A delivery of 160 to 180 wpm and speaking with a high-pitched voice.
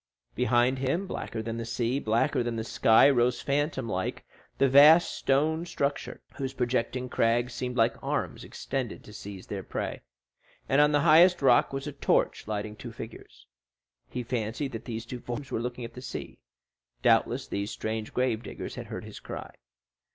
No: average, 175 wpm; low, 125 Hz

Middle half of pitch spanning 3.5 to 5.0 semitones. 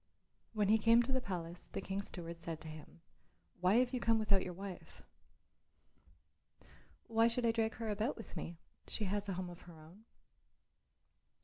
Yes: average, 4.5 semitones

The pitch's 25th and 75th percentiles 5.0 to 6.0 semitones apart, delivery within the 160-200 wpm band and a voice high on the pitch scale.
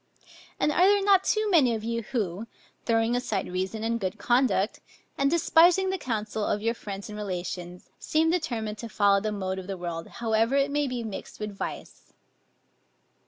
Yes: wide, 5.6 semitones; average, 180 wpm; high, 225 Hz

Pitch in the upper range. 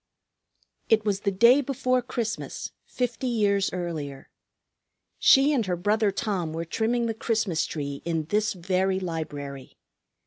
Yes: high, 200 Hz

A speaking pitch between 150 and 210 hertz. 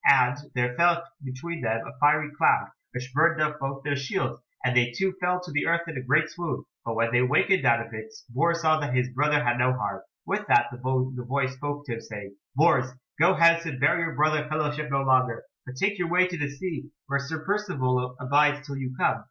No: medium, 140 Hz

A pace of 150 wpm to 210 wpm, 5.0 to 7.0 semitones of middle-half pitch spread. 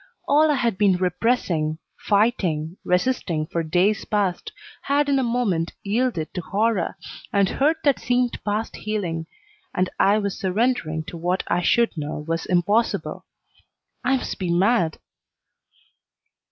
No: average, 140 wpm; wide, 5.6 semitones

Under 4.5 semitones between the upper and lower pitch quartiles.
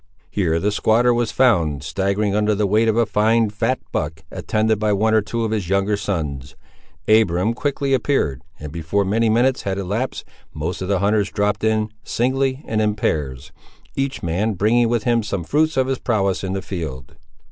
Yes: average, 3.5 semitones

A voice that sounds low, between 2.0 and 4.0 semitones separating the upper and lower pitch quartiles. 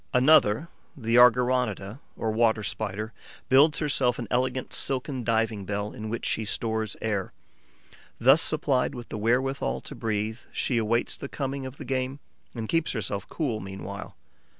Yes: low, 115 Hz; average, 3.3 semitones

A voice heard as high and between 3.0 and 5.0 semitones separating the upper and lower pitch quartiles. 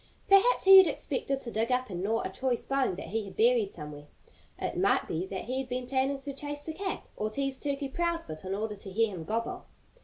No: very high, 250 Hz; wide, 5.4 semitones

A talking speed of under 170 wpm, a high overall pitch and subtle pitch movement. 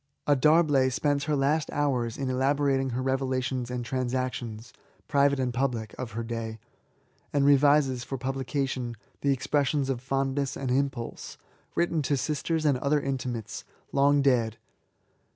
No: average, 150 wpm; low, 135 Hz; narrow, 2.2 semitones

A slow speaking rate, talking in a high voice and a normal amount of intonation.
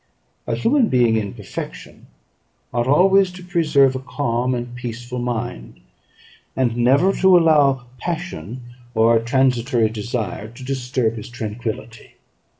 No: slow, 130 wpm; low, 125 Hz; average, 3.5 semitones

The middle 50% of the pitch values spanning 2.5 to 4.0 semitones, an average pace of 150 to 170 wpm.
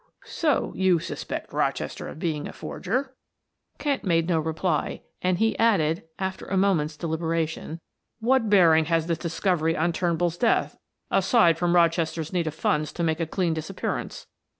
Yes: average, 2.8 semitones; average, 155 wpm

